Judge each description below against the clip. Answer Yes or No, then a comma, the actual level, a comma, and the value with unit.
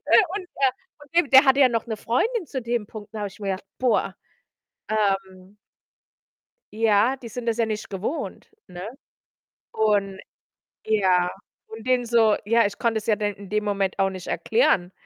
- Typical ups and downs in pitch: Yes, average, 3.3 semitones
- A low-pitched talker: No, high, 215 Hz